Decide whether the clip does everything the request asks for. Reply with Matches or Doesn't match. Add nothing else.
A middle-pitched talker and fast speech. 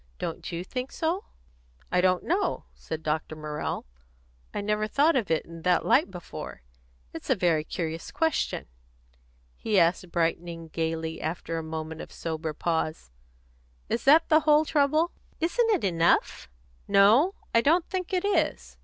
Doesn't match